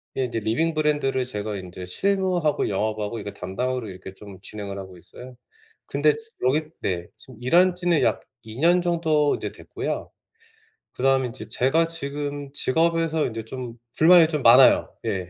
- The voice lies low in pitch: Yes, low, 130 Hz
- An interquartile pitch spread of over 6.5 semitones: Yes, wide, 7.3 semitones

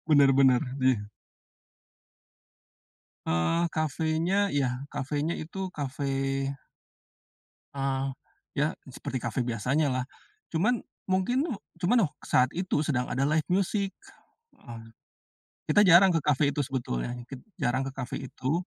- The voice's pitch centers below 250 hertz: Yes, medium, 140 Hz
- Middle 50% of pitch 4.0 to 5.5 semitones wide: Yes, average, 4.5 semitones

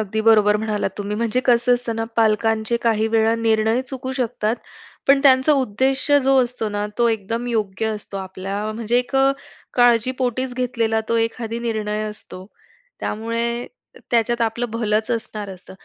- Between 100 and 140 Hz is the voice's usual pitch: No, high, 230 Hz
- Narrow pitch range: Yes, narrow, 2.3 semitones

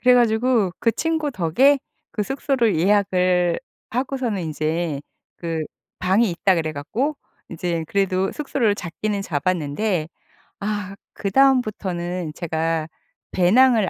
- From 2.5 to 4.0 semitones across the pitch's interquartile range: No, wide, 5.6 semitones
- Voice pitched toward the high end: Yes, high, 195 Hz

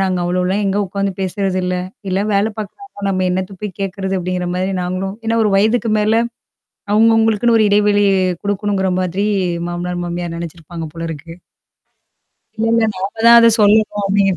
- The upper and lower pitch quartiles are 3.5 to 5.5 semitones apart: No, narrow, 2.4 semitones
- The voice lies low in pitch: No, high, 195 Hz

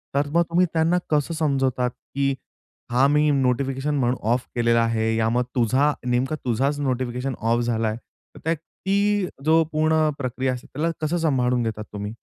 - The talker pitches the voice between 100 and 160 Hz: Yes, low, 135 Hz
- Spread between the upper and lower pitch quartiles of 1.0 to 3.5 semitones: No, average, 4.1 semitones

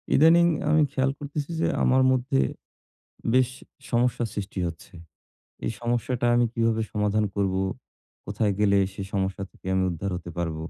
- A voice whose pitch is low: Yes, low, 110 Hz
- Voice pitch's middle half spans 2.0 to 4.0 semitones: No, average, 4.5 semitones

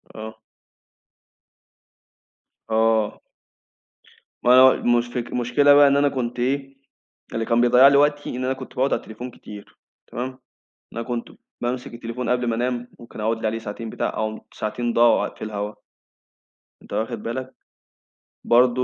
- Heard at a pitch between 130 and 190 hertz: No, low, 120 Hz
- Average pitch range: No, narrow, 2.2 semitones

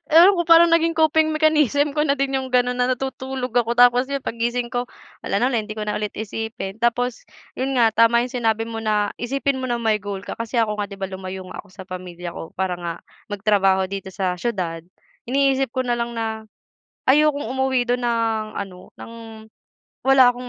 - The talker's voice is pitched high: Yes, high, 235 Hz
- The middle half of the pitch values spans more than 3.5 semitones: Yes, average, 3.9 semitones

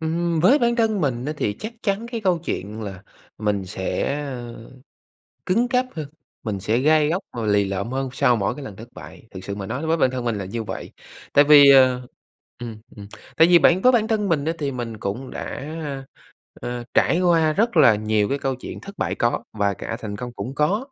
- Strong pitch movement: Yes, wide, 7.4 semitones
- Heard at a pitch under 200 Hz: Yes, low, 135 Hz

